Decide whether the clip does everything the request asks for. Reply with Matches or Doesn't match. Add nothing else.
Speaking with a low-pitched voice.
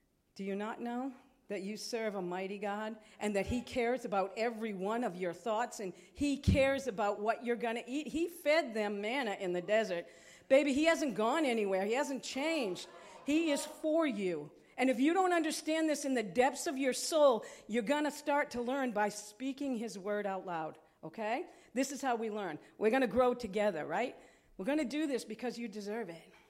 Doesn't match